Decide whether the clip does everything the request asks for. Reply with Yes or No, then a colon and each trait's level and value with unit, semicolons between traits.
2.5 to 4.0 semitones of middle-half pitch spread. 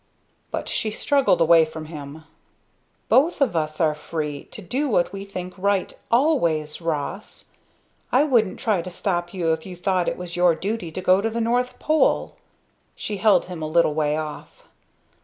No: average, 5.3 semitones